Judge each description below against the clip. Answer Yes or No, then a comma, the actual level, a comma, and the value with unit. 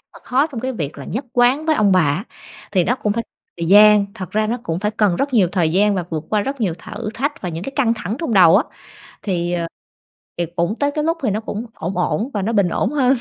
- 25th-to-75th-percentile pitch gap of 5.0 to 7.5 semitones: Yes, wide, 5.5 semitones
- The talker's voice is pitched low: No, high, 210 Hz